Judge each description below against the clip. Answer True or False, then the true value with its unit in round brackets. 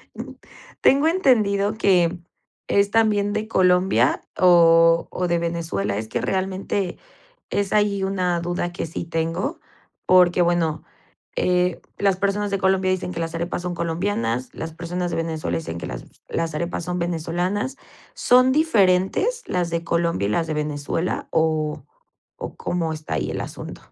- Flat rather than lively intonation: False (3.1 semitones)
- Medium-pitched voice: True (175 Hz)